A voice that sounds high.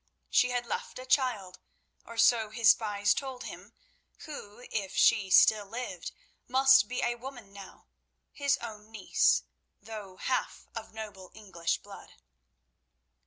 Yes: high, 225 Hz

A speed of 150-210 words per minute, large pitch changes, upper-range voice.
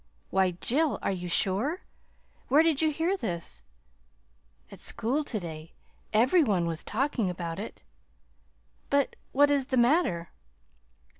No: slow, 135 wpm; wide, 8.3 semitones; high, 235 Hz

